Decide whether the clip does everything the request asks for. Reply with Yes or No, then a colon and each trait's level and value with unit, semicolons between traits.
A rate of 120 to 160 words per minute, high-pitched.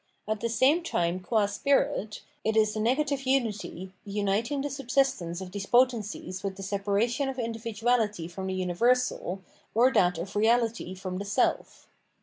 Yes: average, 155 wpm; high, 215 Hz